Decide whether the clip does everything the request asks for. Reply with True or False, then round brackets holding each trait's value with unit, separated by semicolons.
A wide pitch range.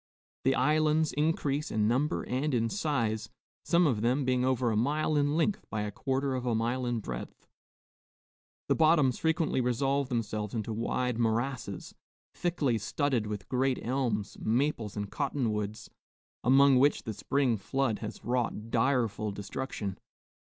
False (4.2 semitones)